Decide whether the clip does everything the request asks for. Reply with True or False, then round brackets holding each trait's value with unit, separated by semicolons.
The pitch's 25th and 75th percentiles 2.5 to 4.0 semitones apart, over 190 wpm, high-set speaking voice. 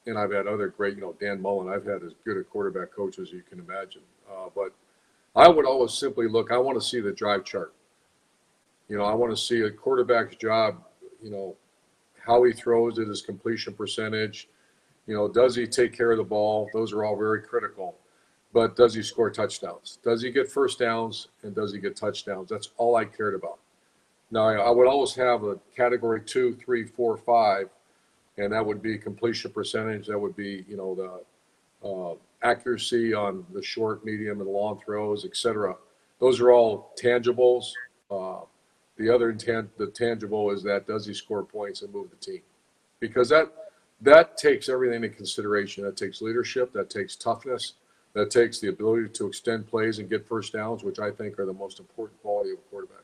False (2.8 semitones; 200 wpm; 115 Hz)